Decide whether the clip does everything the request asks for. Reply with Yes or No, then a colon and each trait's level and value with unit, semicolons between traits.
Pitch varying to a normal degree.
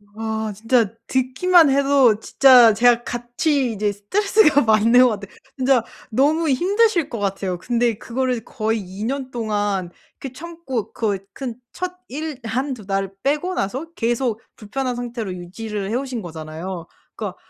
Yes: average, 4.5 semitones